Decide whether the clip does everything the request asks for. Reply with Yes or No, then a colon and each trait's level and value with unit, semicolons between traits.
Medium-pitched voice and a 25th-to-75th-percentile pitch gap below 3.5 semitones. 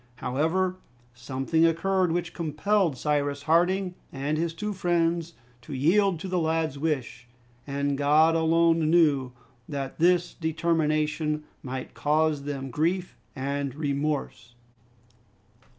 Yes: medium, 155 Hz; average, 3.1 semitones